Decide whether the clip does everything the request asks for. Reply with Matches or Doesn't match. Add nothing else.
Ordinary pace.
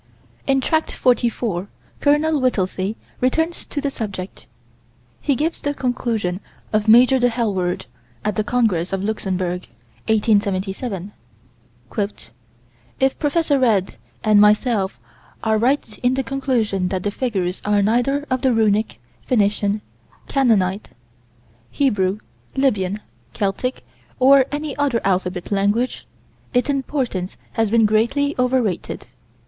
Doesn't match